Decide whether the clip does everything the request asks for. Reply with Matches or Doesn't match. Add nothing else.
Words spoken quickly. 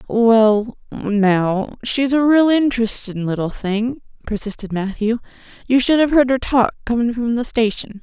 Doesn't match